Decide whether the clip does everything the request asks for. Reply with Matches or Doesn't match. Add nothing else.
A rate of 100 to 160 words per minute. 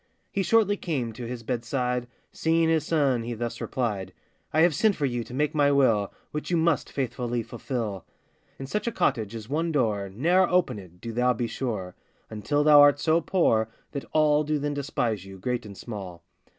Doesn't match